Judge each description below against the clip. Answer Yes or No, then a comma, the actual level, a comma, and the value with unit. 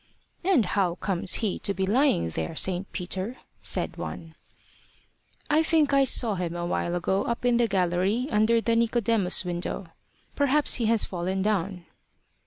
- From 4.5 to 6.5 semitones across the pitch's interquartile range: Yes, average, 4.8 semitones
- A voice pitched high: Yes, high, 200 Hz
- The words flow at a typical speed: Yes, average, 160 wpm